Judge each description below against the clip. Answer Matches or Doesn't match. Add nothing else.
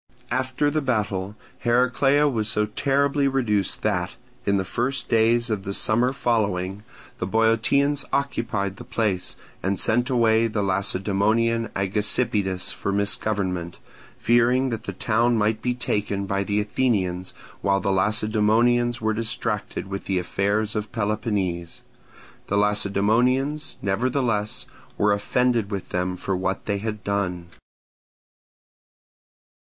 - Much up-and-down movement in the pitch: Doesn't match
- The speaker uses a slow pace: Matches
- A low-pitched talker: Matches